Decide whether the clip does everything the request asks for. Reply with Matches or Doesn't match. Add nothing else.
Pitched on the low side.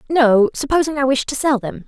Doesn't match